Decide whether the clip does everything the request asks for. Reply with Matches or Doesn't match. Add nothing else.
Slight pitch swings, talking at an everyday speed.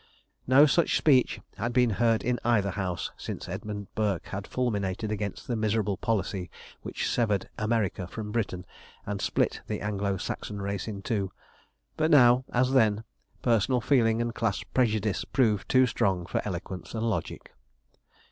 Doesn't match